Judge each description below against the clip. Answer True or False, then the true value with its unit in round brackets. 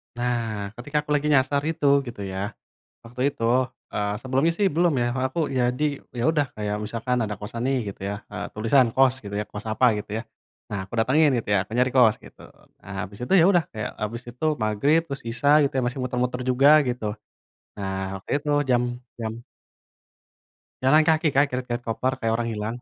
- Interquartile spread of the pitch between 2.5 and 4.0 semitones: False (4.4 semitones)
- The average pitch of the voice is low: True (125 Hz)